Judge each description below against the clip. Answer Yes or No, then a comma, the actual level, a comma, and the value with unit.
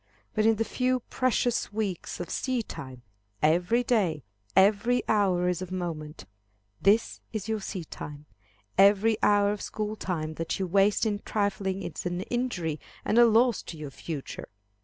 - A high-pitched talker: Yes, high, 200 Hz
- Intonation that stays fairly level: No, average, 4.0 semitones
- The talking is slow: No, average, 155 wpm